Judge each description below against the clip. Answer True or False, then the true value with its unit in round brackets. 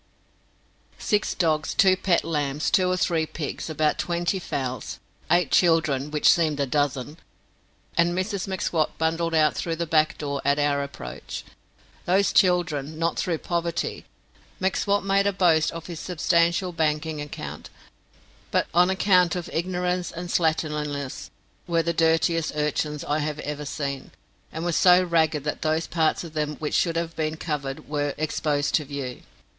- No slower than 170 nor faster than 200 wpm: False (155 wpm)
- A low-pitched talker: False (160 Hz)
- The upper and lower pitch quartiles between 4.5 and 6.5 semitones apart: False (2.6 semitones)